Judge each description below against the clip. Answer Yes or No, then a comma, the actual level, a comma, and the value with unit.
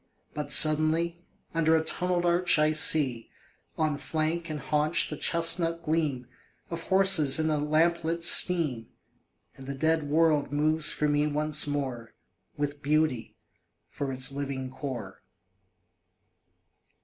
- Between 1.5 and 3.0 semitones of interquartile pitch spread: Yes, narrow, 2.5 semitones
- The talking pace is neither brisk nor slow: No, slow, 125 wpm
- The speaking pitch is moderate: Yes, medium, 155 Hz